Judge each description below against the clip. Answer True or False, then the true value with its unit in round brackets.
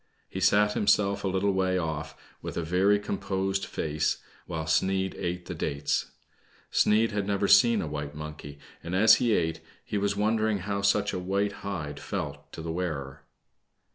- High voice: False (95 Hz)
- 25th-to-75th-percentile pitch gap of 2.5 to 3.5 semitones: False (4.0 semitones)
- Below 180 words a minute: True (170 wpm)